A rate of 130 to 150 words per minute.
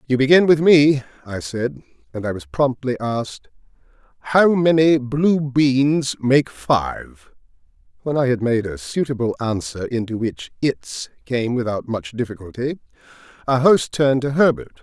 Yes: average, 145 wpm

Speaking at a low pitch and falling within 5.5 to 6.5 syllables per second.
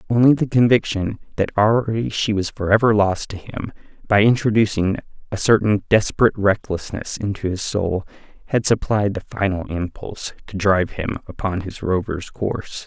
No: low, 105 Hz; 5.1 syllables/s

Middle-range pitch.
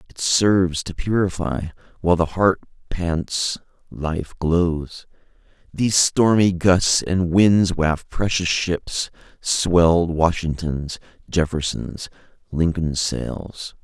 No: very low, 85 Hz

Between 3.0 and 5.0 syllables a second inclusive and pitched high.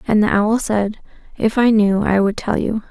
Yes: 4.6 syllables/s; high, 210 Hz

